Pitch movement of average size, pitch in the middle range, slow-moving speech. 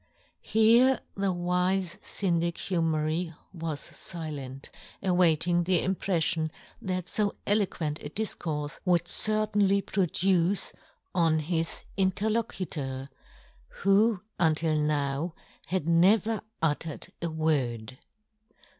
Yes: average, 3.7 semitones; medium, 175 Hz; slow, 100 wpm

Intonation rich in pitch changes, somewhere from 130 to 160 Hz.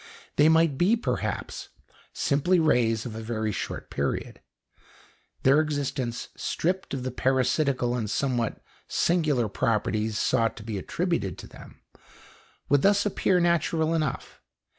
Yes: wide, 6.0 semitones; low, 135 Hz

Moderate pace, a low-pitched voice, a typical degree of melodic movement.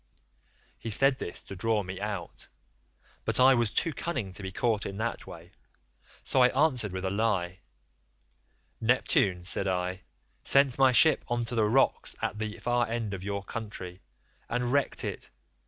Yes: average, 170 wpm; low, 110 Hz; average, 4.3 semitones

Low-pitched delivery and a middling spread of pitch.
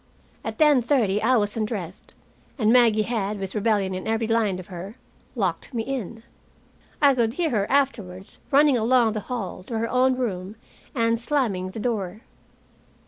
No: high, 225 Hz; average, 4.0 semitones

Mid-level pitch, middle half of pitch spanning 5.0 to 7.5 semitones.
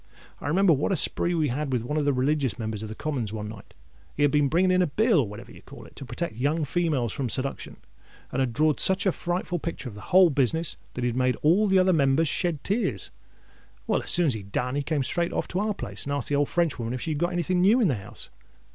Yes: medium, 150 Hz; wide, 5.4 semitones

